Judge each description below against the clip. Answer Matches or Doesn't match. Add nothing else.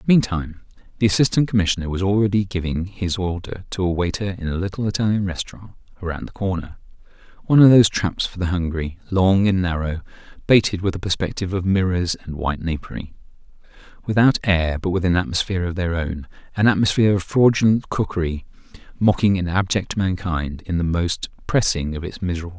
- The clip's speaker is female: Doesn't match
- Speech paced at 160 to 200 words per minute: Matches